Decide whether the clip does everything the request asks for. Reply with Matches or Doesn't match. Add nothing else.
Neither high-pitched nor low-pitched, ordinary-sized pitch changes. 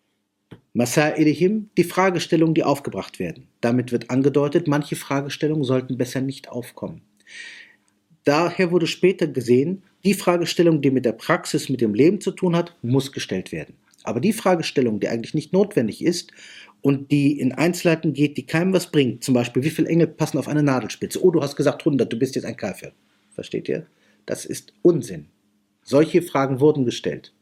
Matches